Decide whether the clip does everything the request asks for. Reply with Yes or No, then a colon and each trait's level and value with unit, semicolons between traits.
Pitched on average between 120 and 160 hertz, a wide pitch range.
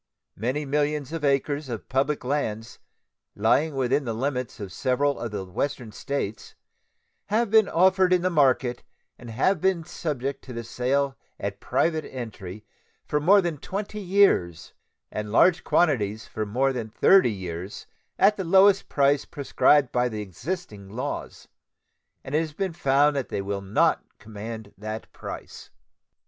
Yes: low, 135 Hz; wide, 6.1 semitones